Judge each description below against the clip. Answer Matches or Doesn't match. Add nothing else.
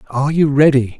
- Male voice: Matches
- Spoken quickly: Doesn't match